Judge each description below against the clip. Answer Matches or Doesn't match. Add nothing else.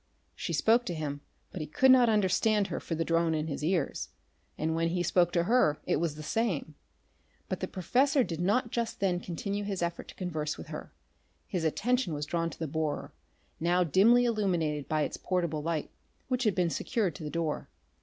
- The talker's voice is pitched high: Doesn't match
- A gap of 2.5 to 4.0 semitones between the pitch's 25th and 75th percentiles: Doesn't match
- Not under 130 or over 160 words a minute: Doesn't match